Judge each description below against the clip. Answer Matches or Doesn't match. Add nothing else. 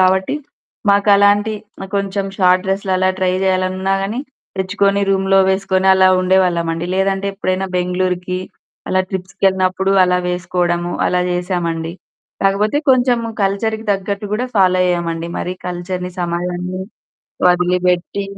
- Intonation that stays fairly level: Matches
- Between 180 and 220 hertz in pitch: Matches